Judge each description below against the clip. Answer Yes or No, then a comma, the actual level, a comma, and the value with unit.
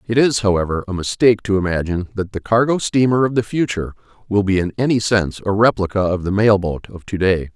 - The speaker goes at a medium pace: No, fast, 220 wpm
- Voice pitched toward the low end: Yes, low, 105 Hz